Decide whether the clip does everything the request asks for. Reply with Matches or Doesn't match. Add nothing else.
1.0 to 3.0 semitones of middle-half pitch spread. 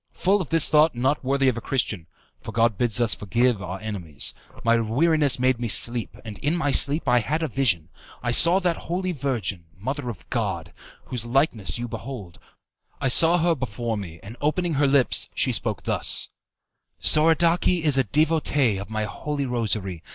Doesn't match